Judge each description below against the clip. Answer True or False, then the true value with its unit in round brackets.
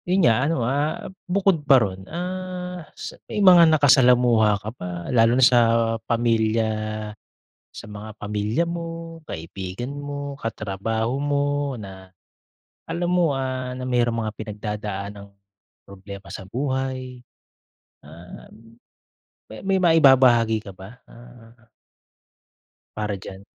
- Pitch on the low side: True (120 Hz)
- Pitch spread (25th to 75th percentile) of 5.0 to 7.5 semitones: True (5.3 semitones)